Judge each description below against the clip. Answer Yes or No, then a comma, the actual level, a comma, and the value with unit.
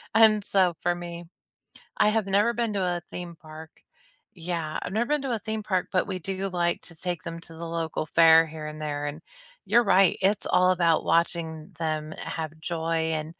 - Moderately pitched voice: Yes, medium, 170 Hz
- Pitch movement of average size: Yes, average, 3.2 semitones